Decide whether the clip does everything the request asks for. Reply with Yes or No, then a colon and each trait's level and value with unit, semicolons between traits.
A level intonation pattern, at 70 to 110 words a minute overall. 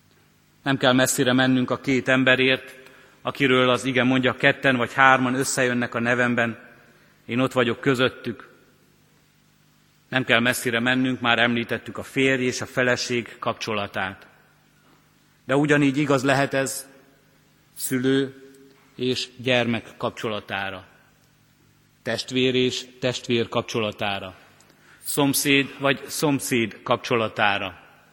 Yes: narrow, 2.3 semitones; slow, 105 wpm